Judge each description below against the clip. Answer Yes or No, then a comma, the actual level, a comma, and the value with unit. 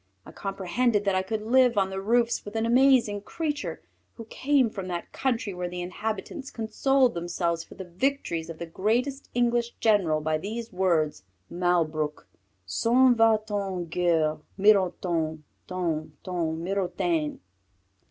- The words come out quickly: No, average, 145 wpm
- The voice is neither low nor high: No, high, 195 Hz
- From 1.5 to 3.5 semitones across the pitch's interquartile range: No, average, 5.3 semitones